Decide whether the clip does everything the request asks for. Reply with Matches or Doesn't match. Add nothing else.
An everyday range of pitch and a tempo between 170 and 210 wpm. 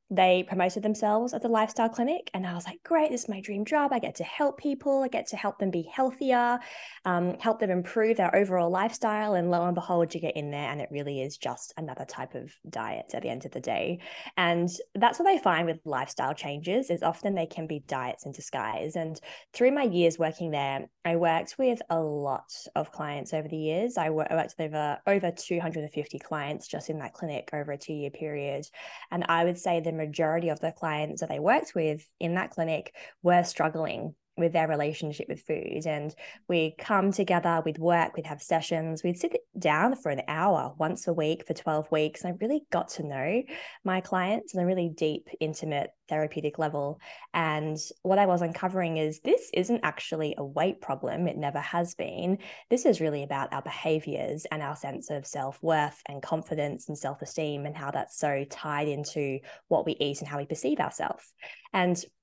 Matches